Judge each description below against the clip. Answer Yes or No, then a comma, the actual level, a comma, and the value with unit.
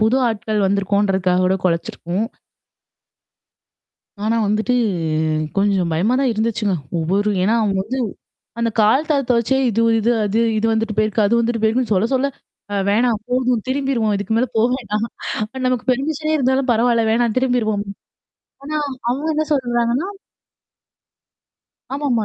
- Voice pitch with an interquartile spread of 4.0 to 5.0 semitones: No, average, 3.4 semitones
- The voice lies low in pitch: No, high, 225 Hz